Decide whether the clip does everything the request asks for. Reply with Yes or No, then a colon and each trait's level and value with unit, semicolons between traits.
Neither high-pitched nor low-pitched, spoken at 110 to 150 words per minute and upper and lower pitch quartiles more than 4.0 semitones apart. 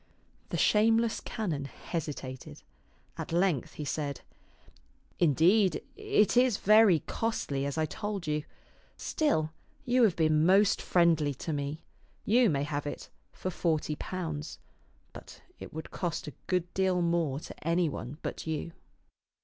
Yes: medium, 165 Hz; average, 140 wpm; average, 4.6 semitones